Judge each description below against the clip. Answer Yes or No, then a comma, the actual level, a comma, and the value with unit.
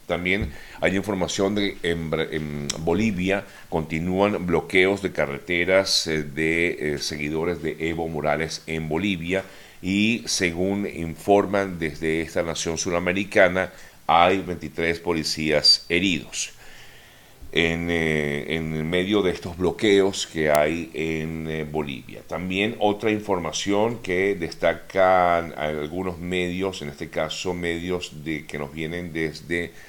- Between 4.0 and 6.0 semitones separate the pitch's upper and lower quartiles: No, average, 3.3 semitones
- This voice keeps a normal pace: No, slow, 110 wpm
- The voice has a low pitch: Yes, very low, 85 Hz